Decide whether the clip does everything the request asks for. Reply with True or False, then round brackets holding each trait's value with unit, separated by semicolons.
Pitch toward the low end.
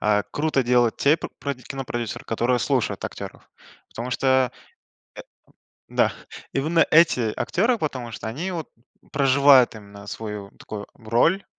True (125 Hz)